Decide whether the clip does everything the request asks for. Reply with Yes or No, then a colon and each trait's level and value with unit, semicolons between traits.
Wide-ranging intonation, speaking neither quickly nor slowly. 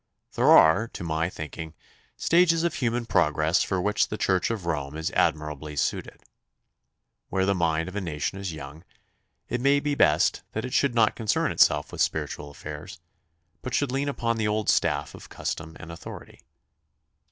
Yes: wide, 6.7 semitones; average, 175 wpm